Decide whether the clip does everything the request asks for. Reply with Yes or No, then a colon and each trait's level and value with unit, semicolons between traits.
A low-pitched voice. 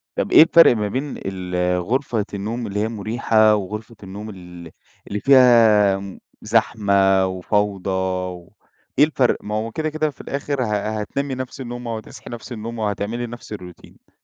Yes: low, 110 Hz